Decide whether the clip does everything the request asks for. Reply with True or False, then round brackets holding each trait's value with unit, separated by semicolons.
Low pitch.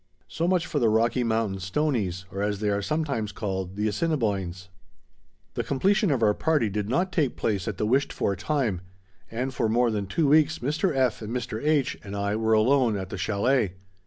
True (115 Hz)